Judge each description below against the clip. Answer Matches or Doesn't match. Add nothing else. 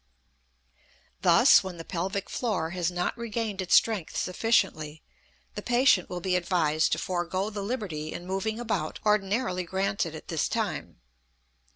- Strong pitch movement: Doesn't match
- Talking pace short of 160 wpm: Matches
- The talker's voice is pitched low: Doesn't match